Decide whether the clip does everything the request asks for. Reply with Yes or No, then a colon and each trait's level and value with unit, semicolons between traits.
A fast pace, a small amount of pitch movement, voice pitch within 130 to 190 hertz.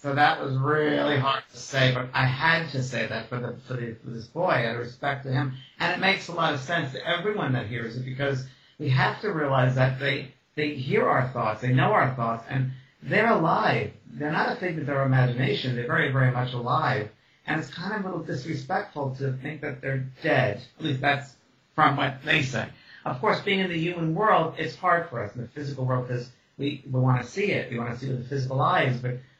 No: fast, 240 wpm; average, 3.1 semitones; low, 135 Hz